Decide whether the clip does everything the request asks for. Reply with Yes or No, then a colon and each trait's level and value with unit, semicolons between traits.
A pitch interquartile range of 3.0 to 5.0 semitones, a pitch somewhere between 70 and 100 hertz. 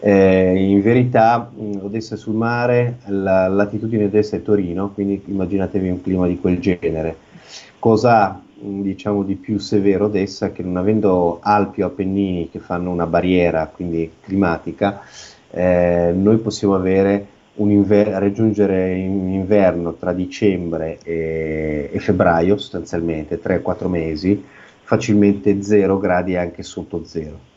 No: narrow, 2.6 semitones; very low, 95 Hz